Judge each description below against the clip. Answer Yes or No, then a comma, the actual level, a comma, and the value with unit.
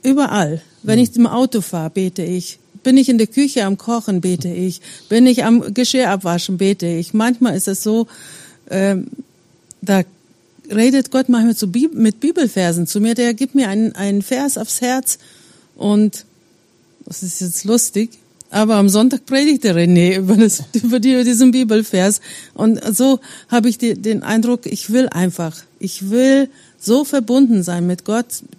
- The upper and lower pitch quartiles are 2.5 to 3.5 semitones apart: No, average, 4.7 semitones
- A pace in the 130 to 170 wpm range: Yes, average, 165 wpm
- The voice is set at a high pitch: Yes, high, 220 Hz